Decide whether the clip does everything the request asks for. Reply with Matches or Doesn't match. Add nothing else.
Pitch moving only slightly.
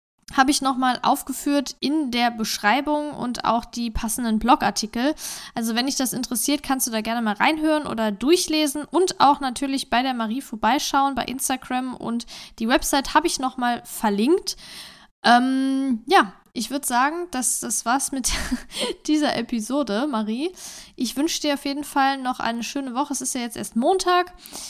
Doesn't match